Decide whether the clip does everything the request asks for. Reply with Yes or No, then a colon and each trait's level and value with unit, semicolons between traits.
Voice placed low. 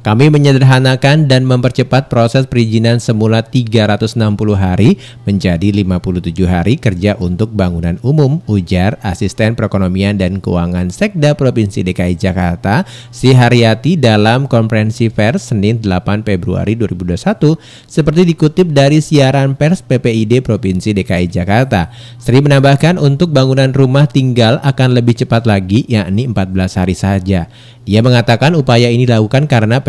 Yes: low, 115 Hz